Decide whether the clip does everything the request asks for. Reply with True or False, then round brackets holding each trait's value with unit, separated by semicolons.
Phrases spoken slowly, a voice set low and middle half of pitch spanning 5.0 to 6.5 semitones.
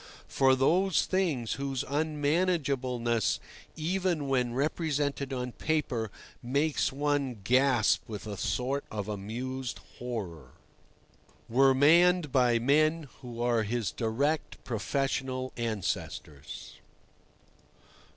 False (95 wpm; 130 Hz; 3.8 semitones)